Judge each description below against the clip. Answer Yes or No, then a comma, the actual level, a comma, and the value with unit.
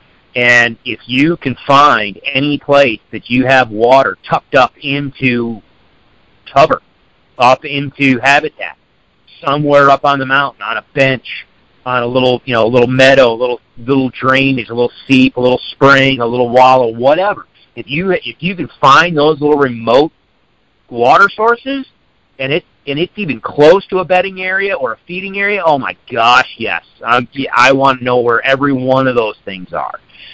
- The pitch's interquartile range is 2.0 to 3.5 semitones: Yes, average, 2.8 semitones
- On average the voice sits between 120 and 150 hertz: Yes, low, 135 Hz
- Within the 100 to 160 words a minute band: No, average, 175 wpm